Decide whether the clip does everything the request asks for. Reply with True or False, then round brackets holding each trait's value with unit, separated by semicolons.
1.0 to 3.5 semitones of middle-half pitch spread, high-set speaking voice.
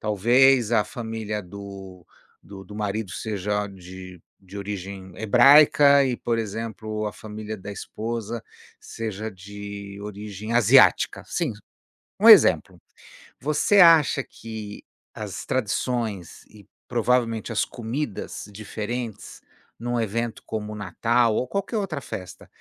False (2.9 semitones; 110 Hz)